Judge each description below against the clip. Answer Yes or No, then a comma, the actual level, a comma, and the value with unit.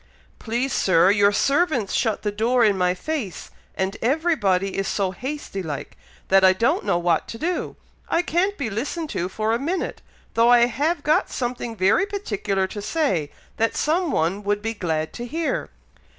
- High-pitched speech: Yes, high, 225 Hz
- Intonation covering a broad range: Yes, wide, 7.5 semitones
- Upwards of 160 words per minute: Yes, average, 180 wpm